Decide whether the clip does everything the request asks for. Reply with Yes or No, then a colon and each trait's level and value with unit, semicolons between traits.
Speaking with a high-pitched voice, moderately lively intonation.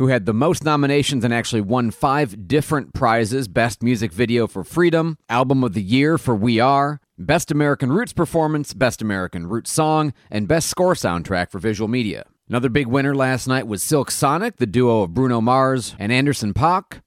No: low, 125 Hz; average, 4.2 semitones